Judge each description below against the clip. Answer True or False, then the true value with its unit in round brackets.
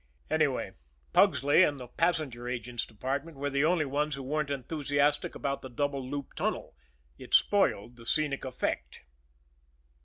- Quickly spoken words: False (145 wpm)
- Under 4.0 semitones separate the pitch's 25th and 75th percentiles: True (2.9 semitones)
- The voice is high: False (140 Hz)